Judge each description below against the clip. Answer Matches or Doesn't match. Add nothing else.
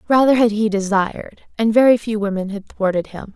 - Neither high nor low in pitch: Doesn't match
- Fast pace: Doesn't match